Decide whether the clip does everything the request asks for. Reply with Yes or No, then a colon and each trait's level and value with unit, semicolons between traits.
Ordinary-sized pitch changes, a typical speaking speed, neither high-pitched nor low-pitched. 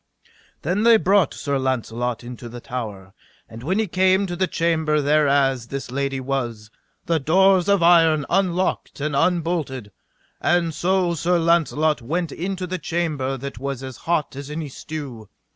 Yes: average, 4.9 semitones; average, 160 wpm; medium, 155 Hz